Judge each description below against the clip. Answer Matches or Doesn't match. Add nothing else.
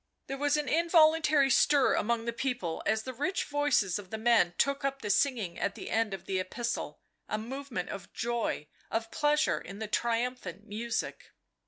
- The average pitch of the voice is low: Doesn't match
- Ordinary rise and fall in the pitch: Matches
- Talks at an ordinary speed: Matches